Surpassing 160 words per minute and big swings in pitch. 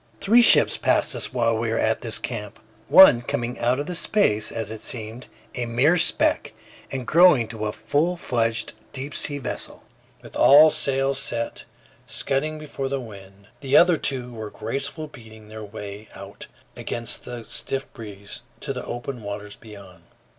No: average, 170 wpm; average, 4.1 semitones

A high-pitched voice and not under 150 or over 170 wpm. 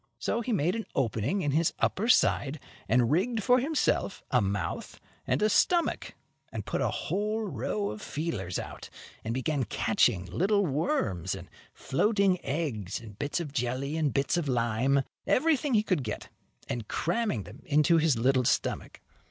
No: medium, 145 Hz; average, 165 wpm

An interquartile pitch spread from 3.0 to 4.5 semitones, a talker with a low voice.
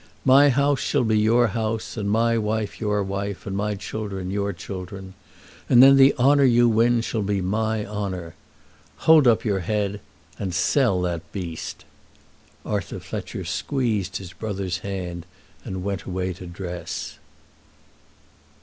Yes: average, 3.5 semitones; low, 105 Hz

